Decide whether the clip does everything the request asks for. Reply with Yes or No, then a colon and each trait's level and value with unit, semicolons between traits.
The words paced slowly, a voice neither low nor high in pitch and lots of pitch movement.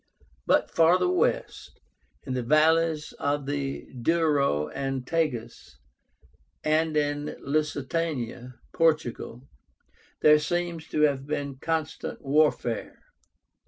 No: slow, 95 wpm; medium, 150 Hz; average, 3.0 semitones